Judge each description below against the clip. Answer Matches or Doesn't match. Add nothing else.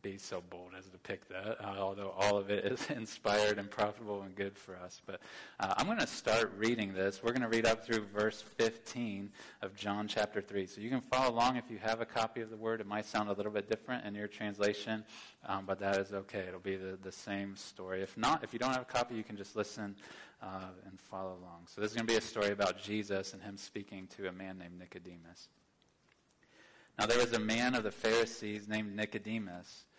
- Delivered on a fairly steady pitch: Matches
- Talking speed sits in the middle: Doesn't match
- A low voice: Matches